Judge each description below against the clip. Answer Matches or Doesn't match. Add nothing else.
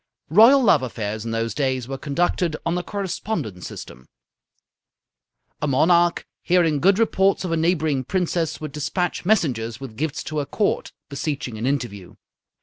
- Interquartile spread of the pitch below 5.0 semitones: Doesn't match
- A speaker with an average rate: Matches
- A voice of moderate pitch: Matches